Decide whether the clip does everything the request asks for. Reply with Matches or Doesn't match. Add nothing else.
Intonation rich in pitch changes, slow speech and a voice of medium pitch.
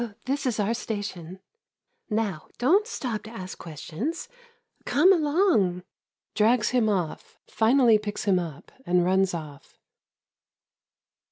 Doesn't match